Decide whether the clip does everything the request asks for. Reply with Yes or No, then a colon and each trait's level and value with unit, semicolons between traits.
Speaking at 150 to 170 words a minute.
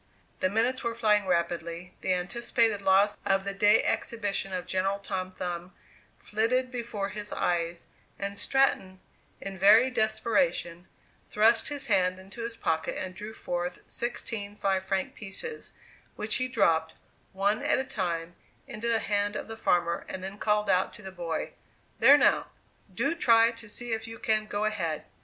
Yes: average, 165 wpm